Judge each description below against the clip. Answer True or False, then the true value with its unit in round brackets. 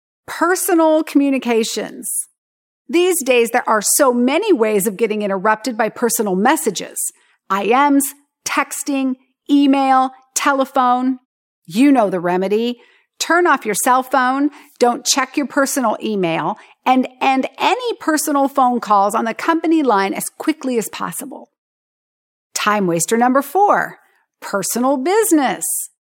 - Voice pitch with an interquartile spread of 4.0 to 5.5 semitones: True (4.5 semitones)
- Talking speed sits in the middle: False (120 wpm)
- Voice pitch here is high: True (260 Hz)